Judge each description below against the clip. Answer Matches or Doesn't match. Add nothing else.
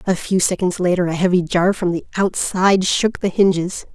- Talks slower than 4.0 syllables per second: Doesn't match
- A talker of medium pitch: Matches